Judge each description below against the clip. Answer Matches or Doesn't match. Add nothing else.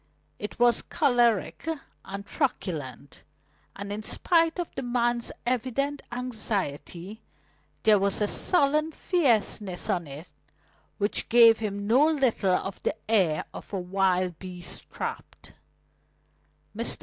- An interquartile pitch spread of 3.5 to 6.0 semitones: Matches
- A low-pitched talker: Doesn't match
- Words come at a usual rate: Doesn't match